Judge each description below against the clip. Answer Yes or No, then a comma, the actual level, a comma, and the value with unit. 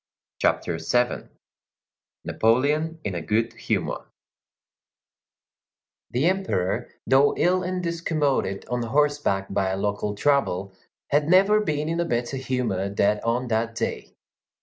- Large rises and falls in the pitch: Yes, wide, 6.8 semitones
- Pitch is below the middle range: Yes, low, 125 Hz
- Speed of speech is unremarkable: No, slow, 120 wpm